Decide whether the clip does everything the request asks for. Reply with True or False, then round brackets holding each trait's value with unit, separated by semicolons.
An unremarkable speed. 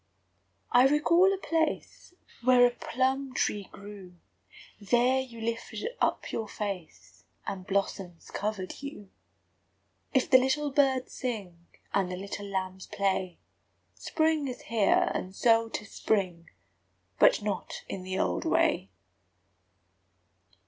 False (120 wpm)